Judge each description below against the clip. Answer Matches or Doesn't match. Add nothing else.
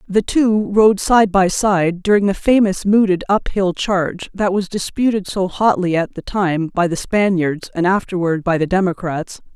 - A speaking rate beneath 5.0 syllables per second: Matches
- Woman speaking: Matches